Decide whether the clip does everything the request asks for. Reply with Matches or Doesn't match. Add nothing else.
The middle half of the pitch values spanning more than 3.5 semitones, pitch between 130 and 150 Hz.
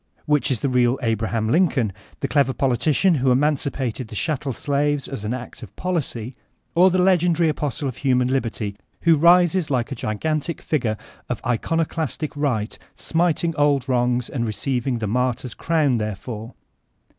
Matches